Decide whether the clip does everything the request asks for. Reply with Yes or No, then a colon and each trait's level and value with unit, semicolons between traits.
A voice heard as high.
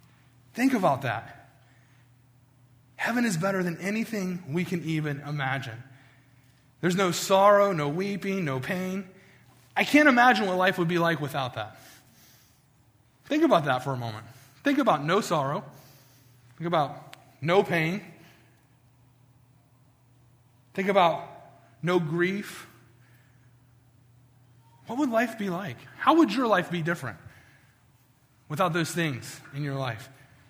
No: low, 135 Hz